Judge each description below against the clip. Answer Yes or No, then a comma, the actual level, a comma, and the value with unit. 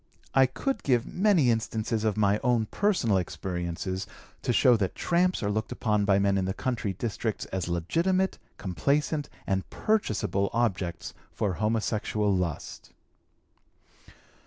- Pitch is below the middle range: Yes, low, 110 Hz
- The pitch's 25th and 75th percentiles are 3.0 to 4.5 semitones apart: No, average, 5.1 semitones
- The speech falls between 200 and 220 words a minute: No, slow, 135 wpm